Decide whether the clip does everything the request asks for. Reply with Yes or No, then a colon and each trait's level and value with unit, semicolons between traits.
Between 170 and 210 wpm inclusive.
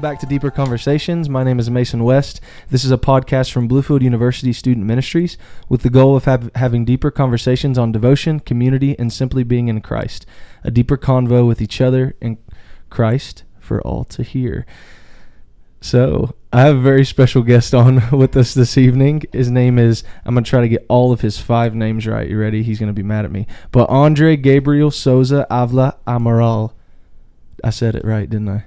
Yes: average, 195 wpm